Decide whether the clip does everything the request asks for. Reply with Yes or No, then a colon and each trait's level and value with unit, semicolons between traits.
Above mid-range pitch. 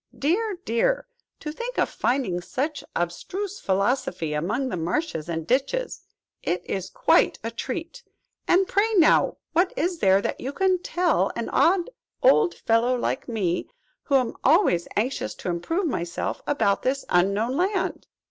Yes: very high, 270 Hz